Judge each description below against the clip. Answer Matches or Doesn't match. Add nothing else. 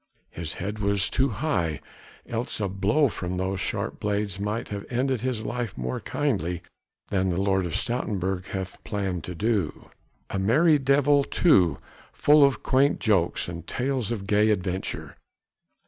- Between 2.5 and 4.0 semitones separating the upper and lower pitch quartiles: Doesn't match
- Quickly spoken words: Doesn't match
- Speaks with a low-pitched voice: Matches